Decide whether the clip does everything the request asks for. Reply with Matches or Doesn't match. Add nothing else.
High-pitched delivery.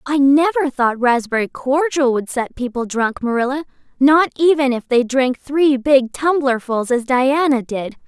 Matches